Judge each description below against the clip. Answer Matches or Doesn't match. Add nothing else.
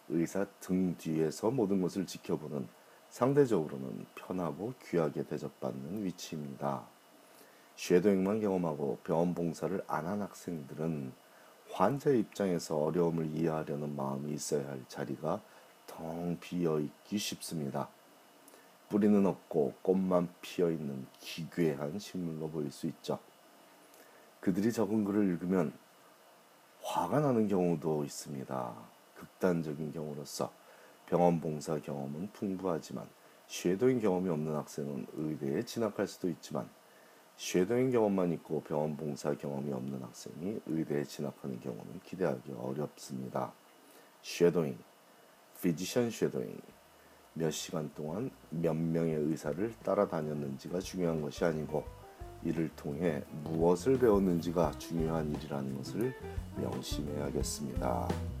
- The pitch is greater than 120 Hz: Doesn't match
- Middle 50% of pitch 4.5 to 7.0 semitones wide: Doesn't match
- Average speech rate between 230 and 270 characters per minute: Doesn't match